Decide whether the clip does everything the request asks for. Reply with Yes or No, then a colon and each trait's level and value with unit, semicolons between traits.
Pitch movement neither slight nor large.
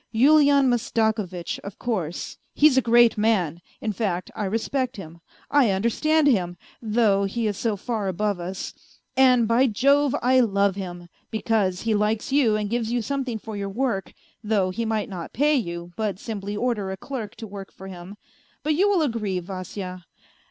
Yes: average, 4.0 semitones